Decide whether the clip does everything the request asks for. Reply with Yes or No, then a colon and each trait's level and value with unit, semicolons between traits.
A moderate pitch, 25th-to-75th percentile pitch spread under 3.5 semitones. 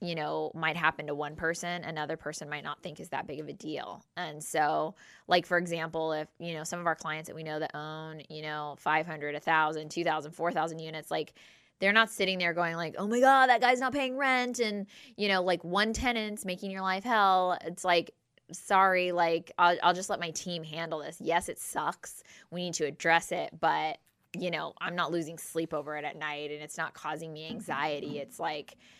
Yes: medium, 165 Hz; average, 3.0 semitones